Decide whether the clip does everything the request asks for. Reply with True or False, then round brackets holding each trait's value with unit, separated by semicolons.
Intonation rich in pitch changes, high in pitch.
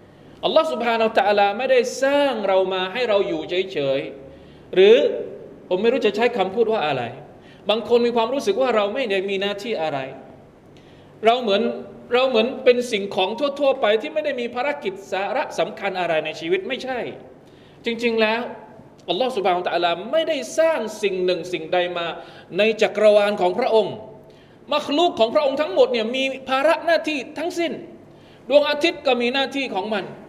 True (6.4 semitones; 225 Hz)